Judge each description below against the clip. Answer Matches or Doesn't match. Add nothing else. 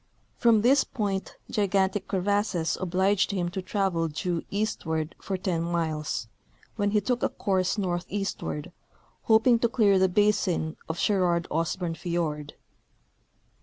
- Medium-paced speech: Doesn't match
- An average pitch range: Matches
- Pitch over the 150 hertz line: Matches